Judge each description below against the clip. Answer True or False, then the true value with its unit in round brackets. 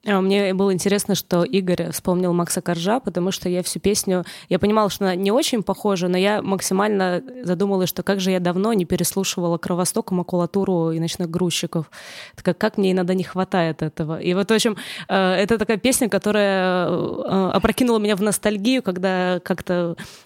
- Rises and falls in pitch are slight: True (2.2 semitones)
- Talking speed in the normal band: False (170 wpm)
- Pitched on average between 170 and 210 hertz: True (190 Hz)